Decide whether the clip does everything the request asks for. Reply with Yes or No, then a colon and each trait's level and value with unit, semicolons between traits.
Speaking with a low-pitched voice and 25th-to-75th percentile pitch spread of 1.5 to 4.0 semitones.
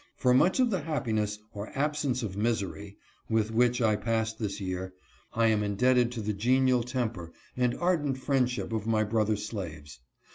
Yes: low, 115 Hz; average, 3.4 semitones